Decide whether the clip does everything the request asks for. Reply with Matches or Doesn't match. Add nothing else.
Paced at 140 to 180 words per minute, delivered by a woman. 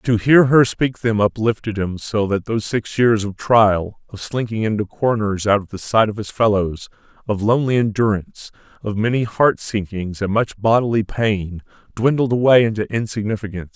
Doesn't match